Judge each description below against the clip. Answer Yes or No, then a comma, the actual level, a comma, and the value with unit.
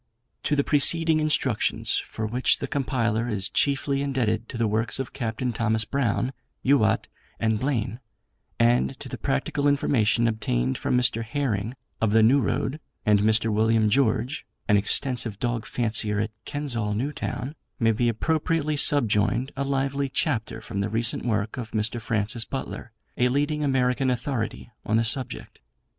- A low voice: Yes, low, 120 Hz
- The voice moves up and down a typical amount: Yes, average, 3.9 semitones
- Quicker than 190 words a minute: No, average, 155 wpm